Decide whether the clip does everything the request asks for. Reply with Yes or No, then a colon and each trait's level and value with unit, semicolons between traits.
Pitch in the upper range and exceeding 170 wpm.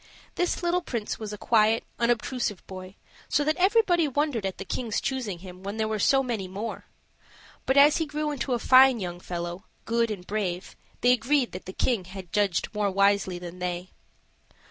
Yes: high, 220 Hz; average, 185 wpm